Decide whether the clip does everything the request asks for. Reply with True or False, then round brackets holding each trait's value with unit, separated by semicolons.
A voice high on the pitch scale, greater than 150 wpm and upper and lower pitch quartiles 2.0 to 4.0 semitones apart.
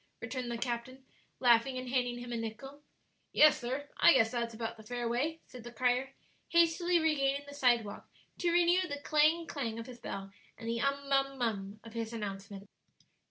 True (250 Hz; 185 wpm; 3.6 semitones)